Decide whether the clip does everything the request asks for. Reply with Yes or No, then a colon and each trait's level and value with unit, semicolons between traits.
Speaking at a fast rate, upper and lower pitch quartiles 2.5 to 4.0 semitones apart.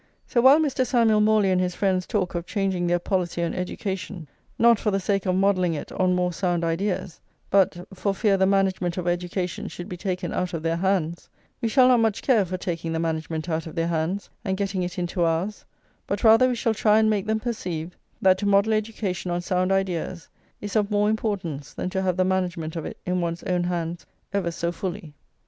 Yes: fast, 215 wpm; average, 2.8 semitones